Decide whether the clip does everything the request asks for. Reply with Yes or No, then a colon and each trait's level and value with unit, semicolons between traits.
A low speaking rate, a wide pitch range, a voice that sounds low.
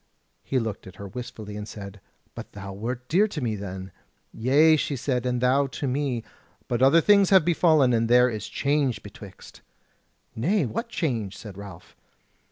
No: average, 175 wpm; wide, 5.7 semitones; low, 125 Hz